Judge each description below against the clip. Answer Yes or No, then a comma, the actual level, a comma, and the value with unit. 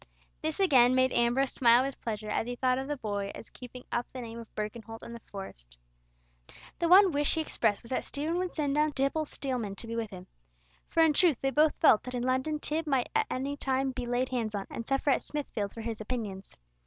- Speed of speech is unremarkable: No, fast, 230 wpm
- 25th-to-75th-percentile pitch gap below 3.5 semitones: No, average, 4.1 semitones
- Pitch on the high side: Yes, very high, 255 Hz